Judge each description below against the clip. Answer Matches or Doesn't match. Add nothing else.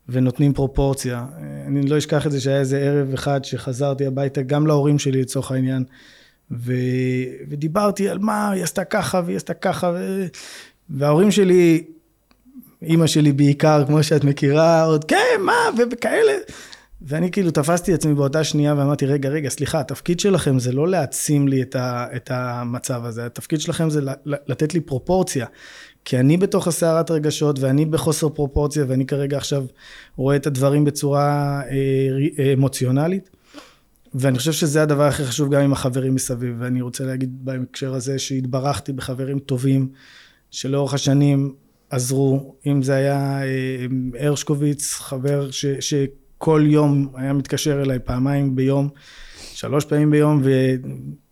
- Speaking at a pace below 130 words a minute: Doesn't match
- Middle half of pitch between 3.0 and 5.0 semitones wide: Doesn't match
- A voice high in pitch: Doesn't match